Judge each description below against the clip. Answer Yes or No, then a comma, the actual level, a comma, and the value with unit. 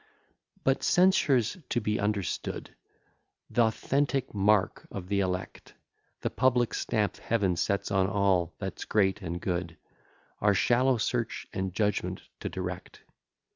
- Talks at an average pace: No, slow, 130 wpm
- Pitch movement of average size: Yes, average, 4.0 semitones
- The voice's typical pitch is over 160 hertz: No, low, 105 Hz